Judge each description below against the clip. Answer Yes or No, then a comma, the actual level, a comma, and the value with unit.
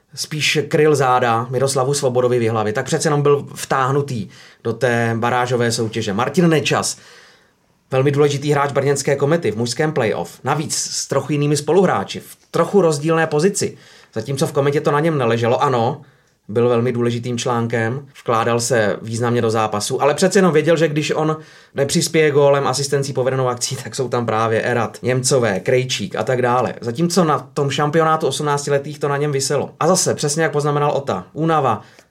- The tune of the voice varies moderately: Yes, average, 3.9 semitones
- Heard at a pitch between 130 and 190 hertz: Yes, medium, 140 Hz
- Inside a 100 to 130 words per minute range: No, average, 165 wpm